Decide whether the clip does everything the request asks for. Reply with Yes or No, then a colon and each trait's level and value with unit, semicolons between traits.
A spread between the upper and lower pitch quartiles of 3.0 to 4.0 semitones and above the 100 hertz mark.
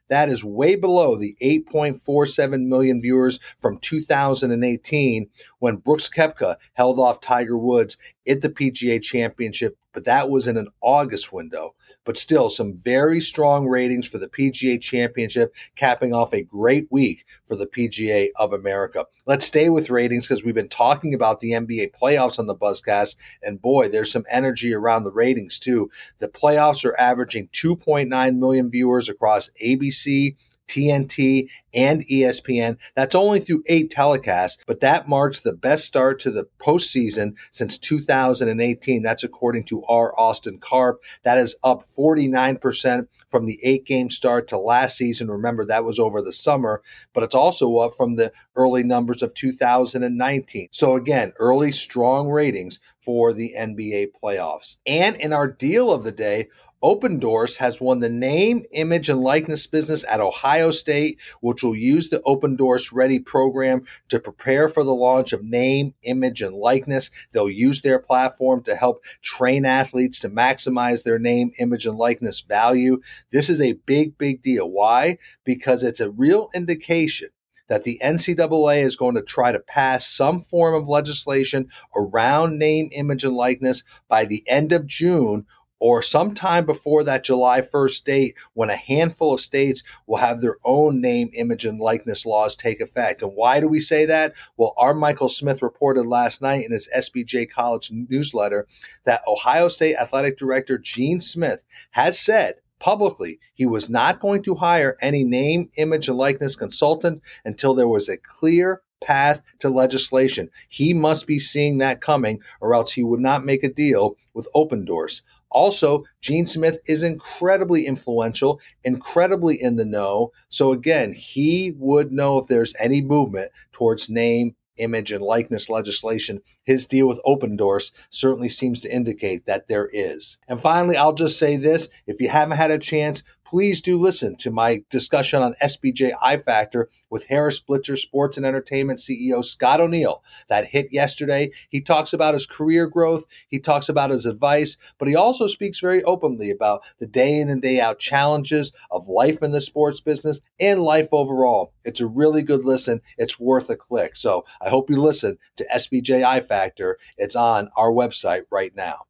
Yes: average, 3.7 semitones; low, 135 Hz